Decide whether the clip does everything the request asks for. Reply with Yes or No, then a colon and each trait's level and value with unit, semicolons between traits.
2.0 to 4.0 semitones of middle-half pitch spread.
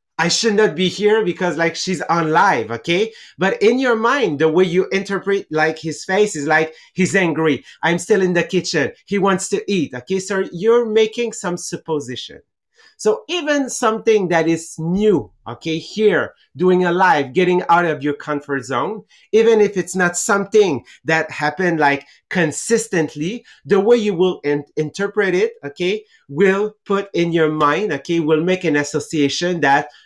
No: average, 4.5 semitones